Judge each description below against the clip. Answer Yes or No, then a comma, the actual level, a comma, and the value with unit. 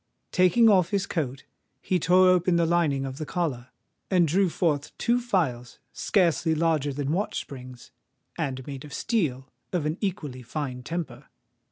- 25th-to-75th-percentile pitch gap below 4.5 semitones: No, average, 5.1 semitones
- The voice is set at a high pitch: No, medium, 160 Hz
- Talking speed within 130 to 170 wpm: Yes, average, 160 wpm